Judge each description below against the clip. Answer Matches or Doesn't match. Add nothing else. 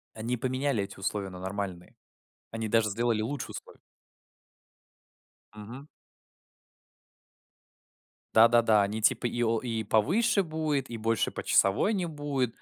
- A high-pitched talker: Doesn't match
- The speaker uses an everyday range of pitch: Matches